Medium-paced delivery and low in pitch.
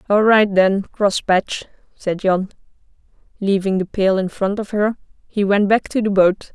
No: average, 175 wpm; high, 200 Hz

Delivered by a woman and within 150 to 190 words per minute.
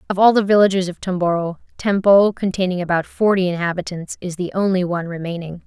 Yes: female; average, 170 wpm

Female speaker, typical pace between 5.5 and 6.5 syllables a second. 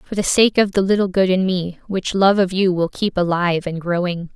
No: female; 5.2 syllables/s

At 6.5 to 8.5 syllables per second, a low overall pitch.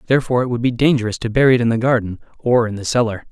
Yes: 7.9 syllables/s; low, 120 Hz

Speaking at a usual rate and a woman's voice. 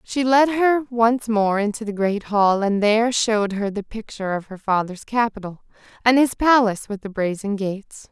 Yes: average, 190 wpm; female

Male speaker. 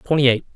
Yes: male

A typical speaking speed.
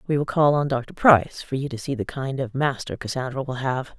No: fast, 255 wpm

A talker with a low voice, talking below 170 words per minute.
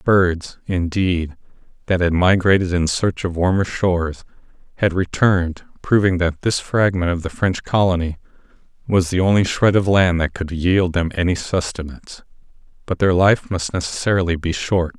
Yes: very low, 90 Hz; average, 155 wpm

